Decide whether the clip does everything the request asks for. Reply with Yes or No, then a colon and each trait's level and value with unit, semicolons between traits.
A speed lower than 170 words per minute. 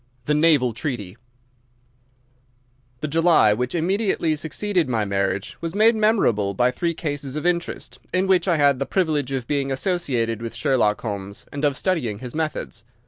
Yes: average, 160 wpm